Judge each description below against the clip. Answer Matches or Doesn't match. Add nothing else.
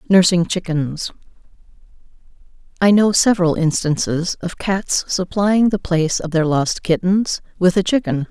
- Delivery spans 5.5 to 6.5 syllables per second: Doesn't match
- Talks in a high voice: Doesn't match